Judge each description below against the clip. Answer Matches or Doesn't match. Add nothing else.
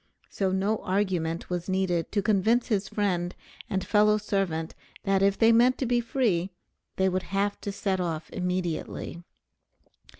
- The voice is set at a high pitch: Matches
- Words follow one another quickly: Doesn't match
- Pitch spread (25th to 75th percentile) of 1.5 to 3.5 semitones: Matches